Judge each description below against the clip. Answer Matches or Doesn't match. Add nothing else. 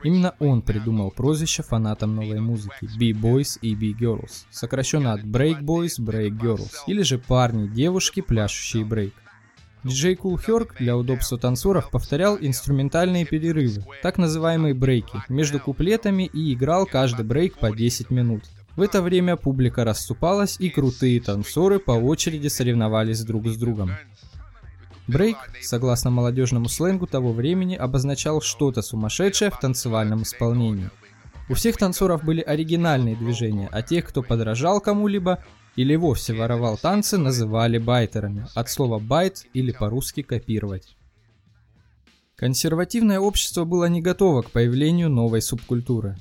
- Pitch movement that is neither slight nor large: Doesn't match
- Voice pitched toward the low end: Matches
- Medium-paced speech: Matches